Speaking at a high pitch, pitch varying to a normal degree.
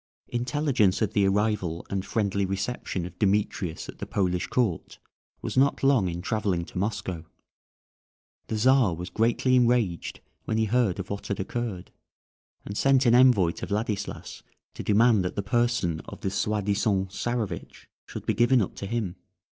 No: low, 105 Hz; average, 4.0 semitones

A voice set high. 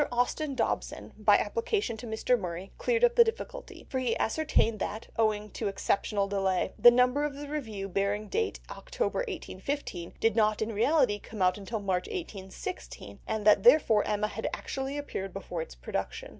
Yes: high, 220 Hz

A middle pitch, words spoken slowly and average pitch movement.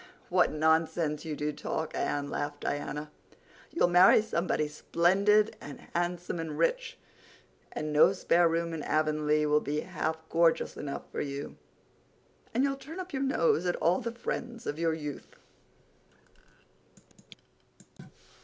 Yes: medium, 165 Hz; slow, 130 wpm; average, 3.4 semitones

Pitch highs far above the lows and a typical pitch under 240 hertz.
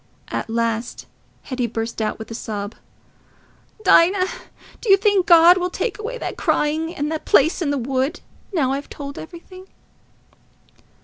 No: wide, 6.8 semitones; very high, 300 Hz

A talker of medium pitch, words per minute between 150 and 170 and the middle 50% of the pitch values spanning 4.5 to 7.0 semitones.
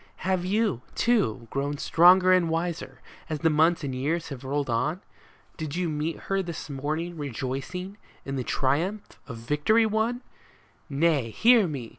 Yes: medium, 160 Hz; average, 160 wpm; average, 4.9 semitones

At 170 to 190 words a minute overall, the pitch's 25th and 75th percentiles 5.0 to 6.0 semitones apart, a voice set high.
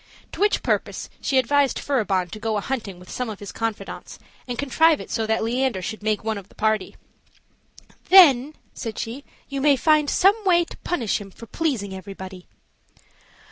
Yes: average, 180 wpm; wide, 5.6 semitones; high, 230 Hz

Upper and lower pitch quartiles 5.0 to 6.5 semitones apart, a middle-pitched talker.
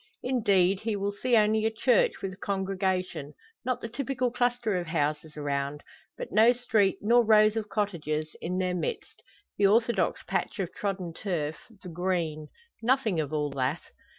No: wide, 5.4 semitones; high, 195 Hz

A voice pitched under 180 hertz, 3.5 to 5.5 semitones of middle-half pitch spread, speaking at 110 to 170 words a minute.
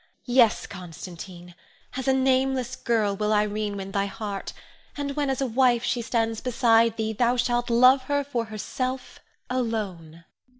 No: high, 230 Hz; average, 3.8 semitones; average, 155 wpm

